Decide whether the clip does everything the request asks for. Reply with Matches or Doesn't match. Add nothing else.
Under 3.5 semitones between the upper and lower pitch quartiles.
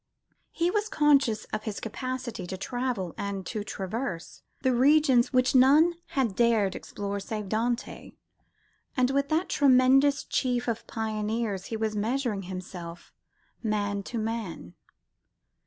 Doesn't match